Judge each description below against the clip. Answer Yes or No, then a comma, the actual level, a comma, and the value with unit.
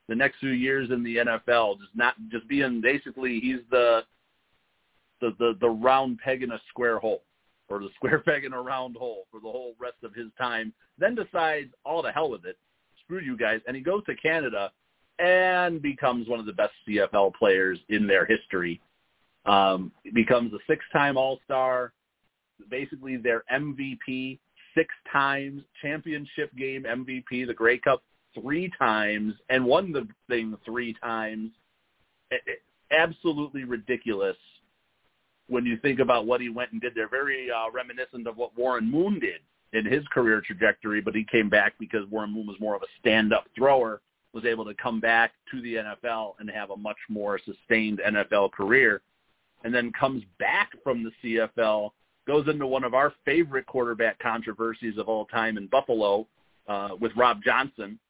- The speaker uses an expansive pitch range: No, average, 3.1 semitones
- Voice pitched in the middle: No, low, 120 Hz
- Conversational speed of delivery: Yes, average, 175 wpm